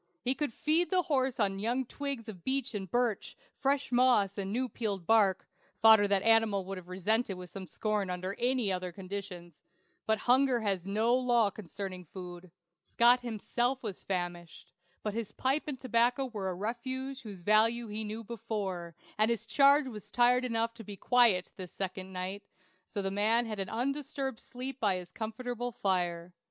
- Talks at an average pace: Yes, average, 175 wpm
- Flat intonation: No, average, 4.2 semitones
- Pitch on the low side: No, high, 220 Hz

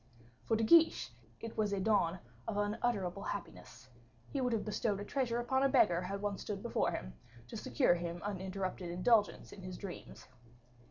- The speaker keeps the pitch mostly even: No, average, 3.8 semitones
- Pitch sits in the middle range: No, high, 205 Hz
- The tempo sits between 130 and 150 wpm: No, average, 175 wpm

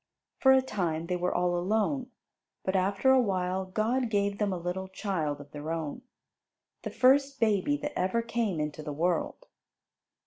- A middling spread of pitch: Yes, average, 4.9 semitones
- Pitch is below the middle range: No, high, 190 Hz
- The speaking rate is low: No, average, 170 wpm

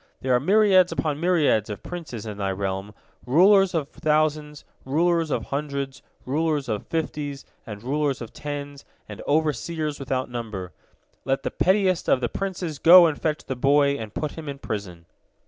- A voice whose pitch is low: No, medium, 145 Hz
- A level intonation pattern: No, average, 4.7 semitones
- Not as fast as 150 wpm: No, average, 165 wpm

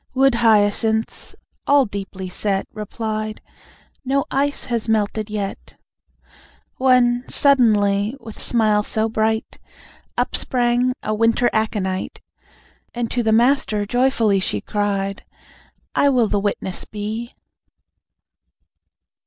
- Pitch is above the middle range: Yes, high, 220 Hz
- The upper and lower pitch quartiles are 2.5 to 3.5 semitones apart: Yes, average, 2.8 semitones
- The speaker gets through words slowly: Yes, slow, 105 wpm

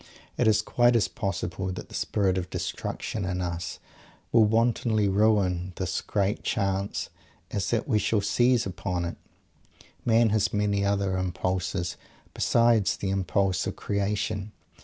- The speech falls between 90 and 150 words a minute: Yes, average, 140 wpm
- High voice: No, low, 100 Hz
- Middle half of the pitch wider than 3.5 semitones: No, average, 2.8 semitones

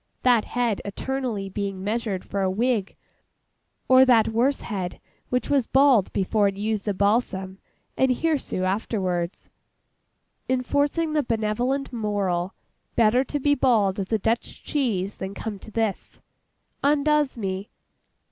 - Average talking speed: No, slow, 130 wpm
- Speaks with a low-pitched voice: No, high, 220 Hz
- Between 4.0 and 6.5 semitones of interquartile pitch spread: Yes, average, 4.7 semitones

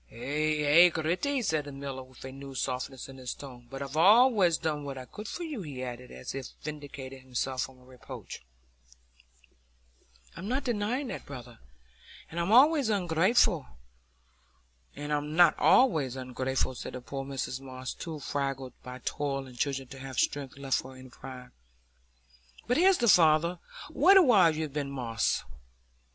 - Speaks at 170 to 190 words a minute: No, average, 155 wpm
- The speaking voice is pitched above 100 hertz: Yes, medium, 140 Hz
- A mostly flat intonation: No, average, 4.7 semitones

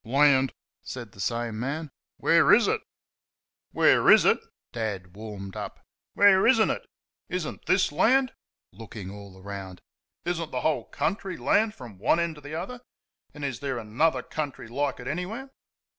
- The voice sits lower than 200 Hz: Yes, medium, 140 Hz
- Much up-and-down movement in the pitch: Yes, wide, 8.1 semitones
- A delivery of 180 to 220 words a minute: No, average, 170 wpm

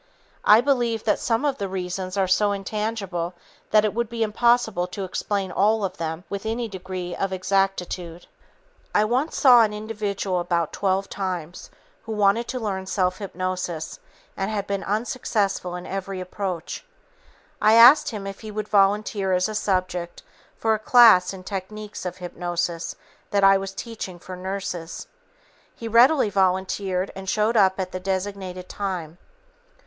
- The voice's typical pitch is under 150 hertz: No, high, 195 Hz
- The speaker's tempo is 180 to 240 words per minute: No, average, 160 wpm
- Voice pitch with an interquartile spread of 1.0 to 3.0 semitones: Yes, narrow, 2.6 semitones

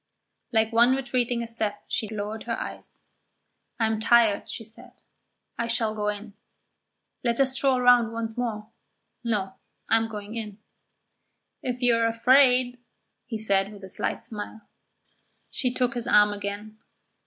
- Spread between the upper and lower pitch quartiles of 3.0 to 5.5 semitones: No, narrow, 2.4 semitones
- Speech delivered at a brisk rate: No, average, 155 wpm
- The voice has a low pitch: No, high, 225 Hz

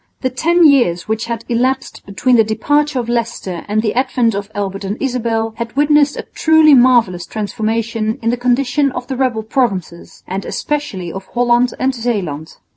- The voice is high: Yes, high, 235 Hz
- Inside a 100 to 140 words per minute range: No, average, 175 wpm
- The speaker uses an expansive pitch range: No, average, 3.5 semitones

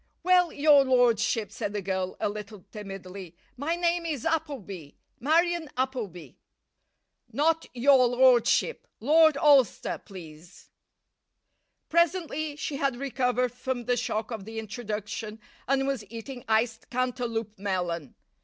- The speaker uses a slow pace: Yes, slow, 120 wpm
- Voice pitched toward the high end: Yes, high, 245 Hz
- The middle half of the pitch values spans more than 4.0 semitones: Yes, average, 5.3 semitones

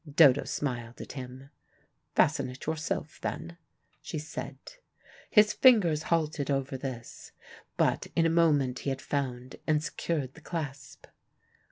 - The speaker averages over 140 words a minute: No, slow, 135 wpm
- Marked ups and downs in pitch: No, average, 3.6 semitones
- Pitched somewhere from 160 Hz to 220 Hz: No, medium, 145 Hz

